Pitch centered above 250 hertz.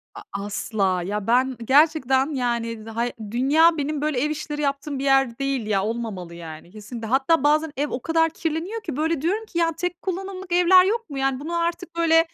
Yes: very high, 285 Hz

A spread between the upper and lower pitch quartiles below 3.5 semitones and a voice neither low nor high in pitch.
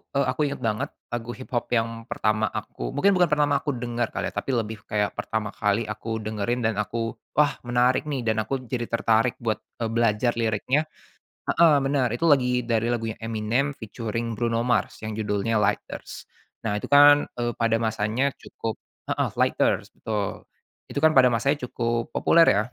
No: average, 2.8 semitones; low, 115 Hz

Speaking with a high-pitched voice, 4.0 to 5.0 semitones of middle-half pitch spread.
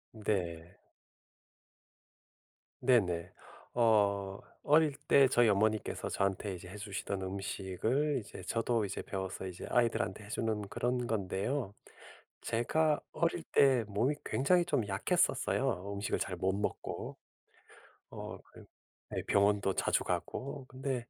No: low, 105 Hz; average, 4.5 semitones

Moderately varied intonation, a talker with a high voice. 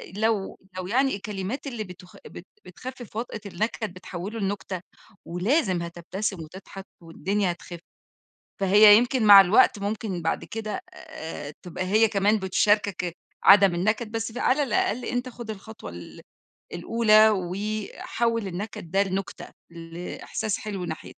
Yes: average, 3.4 semitones; high, 205 Hz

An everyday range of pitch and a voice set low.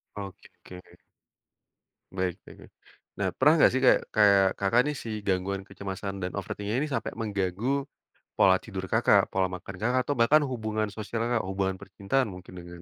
Yes: average, 3.3 semitones; low, 100 Hz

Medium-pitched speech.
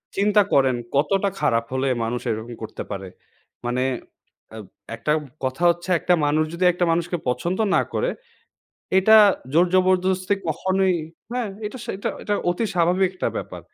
Yes: medium, 175 Hz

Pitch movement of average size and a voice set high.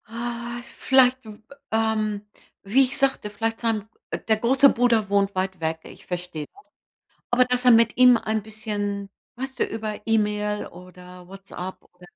Yes: average, 3.2 semitones; high, 220 Hz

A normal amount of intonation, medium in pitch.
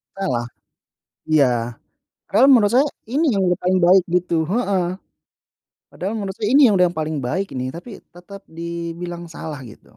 Yes: average, 3.0 semitones; medium, 180 Hz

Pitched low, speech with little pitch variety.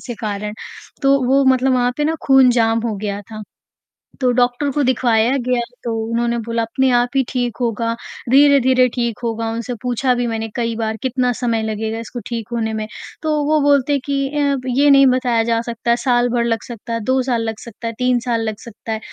No: high, 240 Hz; narrow, 2.2 semitones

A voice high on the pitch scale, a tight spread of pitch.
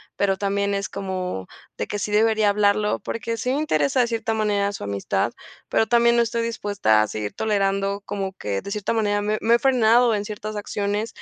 Yes: high, 205 Hz; narrow, 2.2 semitones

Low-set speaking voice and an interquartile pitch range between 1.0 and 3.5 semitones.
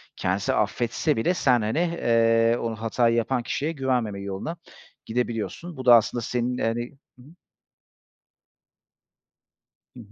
Yes: low, 120 Hz; narrow, 2.5 semitones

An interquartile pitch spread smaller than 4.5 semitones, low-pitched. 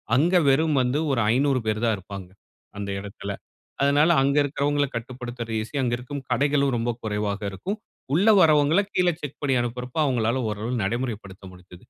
No: average, 4.8 semitones; low, 125 Hz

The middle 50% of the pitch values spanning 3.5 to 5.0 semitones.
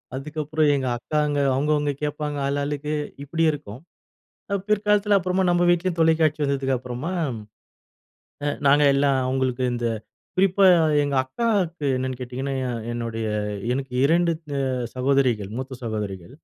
Yes: average, 3.8 semitones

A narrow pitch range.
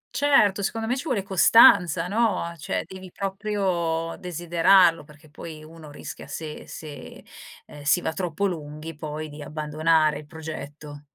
No: average, 3.9 semitones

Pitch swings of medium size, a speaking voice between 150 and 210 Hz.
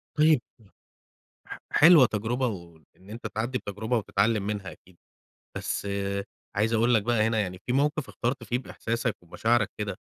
No: average, 3.4 semitones; low, 110 Hz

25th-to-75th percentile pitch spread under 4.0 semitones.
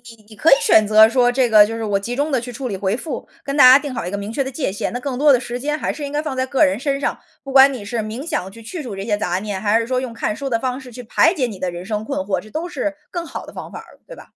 No: average, 4.4 semitones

